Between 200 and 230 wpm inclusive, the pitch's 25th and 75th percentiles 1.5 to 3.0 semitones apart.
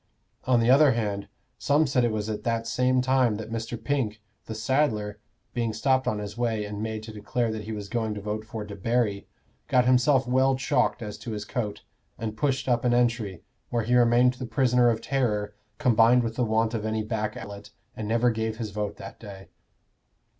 Yes: fast, 205 wpm; average, 2.7 semitones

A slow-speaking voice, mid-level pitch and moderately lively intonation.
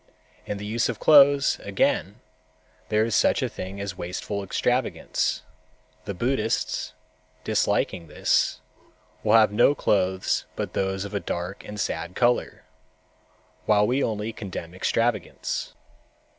No: slow, 130 wpm; low, 105 Hz; average, 3.4 semitones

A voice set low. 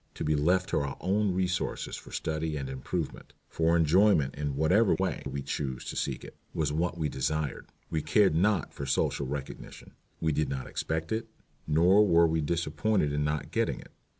Yes: very low, 80 Hz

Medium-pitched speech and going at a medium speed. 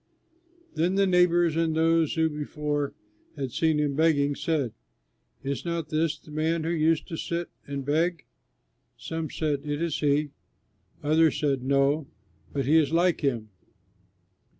Yes: medium, 155 Hz; average, 150 wpm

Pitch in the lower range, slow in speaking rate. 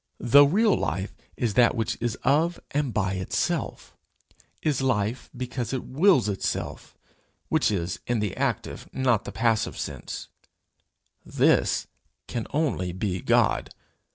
Yes: low, 120 Hz; slow, 130 wpm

